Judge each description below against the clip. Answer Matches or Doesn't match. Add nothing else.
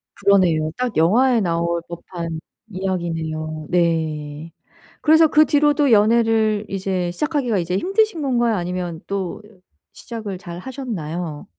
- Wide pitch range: Matches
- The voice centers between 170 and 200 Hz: Matches